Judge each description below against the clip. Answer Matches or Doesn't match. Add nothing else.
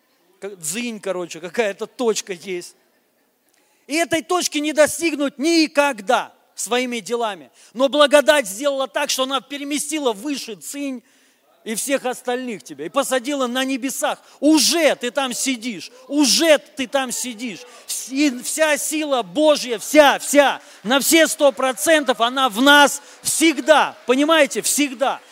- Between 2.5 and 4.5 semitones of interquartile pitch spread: Matches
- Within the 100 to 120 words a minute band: Doesn't match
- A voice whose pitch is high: Matches